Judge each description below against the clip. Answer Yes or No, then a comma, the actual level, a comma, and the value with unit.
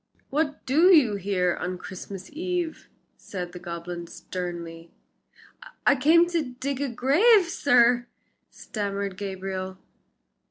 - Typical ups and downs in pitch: No, wide, 7.8 semitones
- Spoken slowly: Yes, slow, 115 wpm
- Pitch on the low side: No, high, 210 Hz